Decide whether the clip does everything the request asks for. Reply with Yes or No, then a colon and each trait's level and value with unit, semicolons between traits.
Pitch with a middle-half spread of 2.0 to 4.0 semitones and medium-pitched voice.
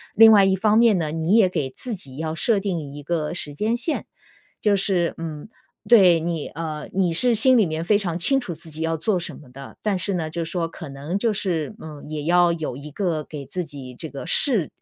No: average, 4.6 semitones; medium, 170 Hz